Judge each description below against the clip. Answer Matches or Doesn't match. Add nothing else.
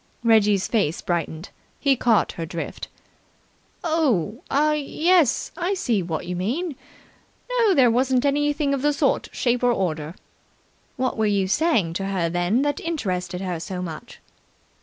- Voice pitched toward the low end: Doesn't match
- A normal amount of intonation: Doesn't match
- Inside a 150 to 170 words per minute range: Matches